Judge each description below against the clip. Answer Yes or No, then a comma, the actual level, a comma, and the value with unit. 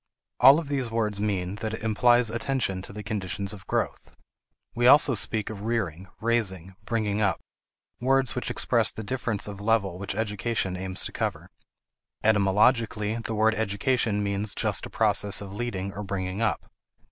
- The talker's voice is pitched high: No, low, 105 Hz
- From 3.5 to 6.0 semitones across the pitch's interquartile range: No, average, 2.9 semitones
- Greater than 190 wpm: No, average, 165 wpm